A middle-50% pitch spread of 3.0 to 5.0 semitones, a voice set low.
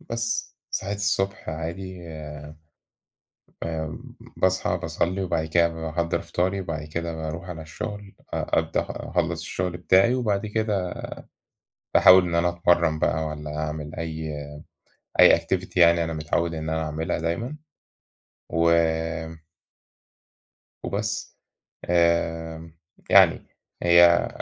No: narrow, 2.5 semitones; very low, 85 Hz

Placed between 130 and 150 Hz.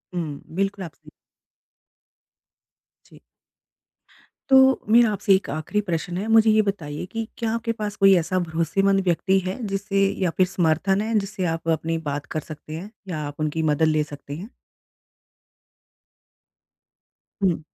No: medium, 185 Hz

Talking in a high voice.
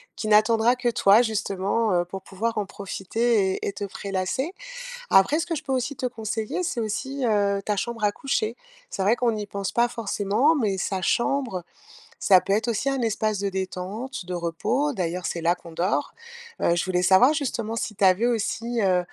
Yes: high, 215 Hz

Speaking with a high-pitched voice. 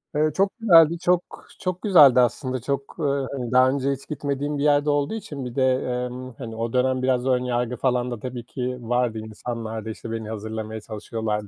No: low, 125 Hz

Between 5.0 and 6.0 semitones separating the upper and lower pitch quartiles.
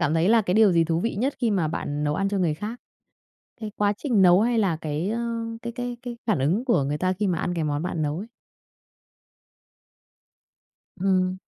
Yes: wide, 5.5 semitones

